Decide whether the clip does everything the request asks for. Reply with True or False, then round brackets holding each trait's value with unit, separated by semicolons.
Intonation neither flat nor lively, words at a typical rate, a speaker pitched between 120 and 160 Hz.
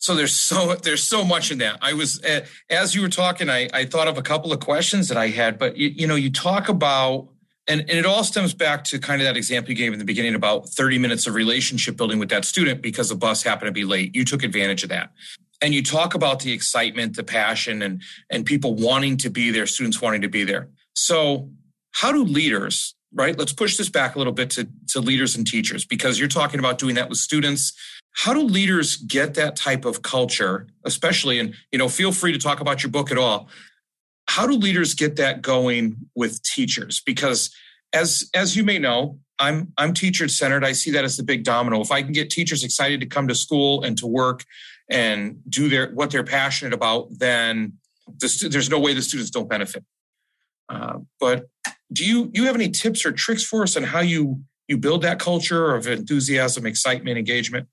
False (4.8 semitones; 220 wpm; 140 Hz)